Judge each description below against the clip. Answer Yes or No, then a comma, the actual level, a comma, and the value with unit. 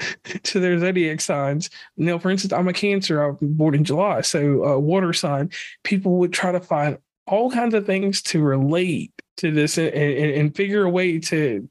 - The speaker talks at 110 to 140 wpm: No, average, 200 wpm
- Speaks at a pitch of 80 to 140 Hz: No, medium, 175 Hz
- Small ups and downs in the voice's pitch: No, average, 4.3 semitones